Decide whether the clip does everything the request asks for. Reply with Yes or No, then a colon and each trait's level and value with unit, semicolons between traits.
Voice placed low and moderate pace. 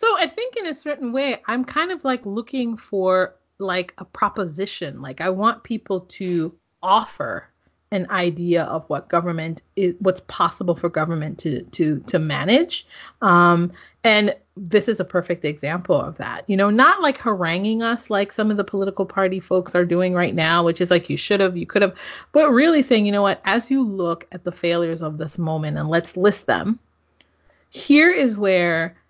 No: high, 190 Hz; average, 190 wpm